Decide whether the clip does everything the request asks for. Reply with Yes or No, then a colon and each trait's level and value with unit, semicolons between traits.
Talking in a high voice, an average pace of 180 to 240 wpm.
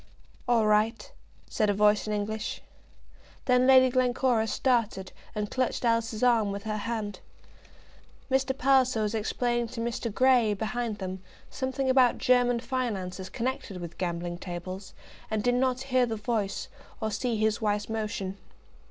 No: high, 225 Hz; average, 150 wpm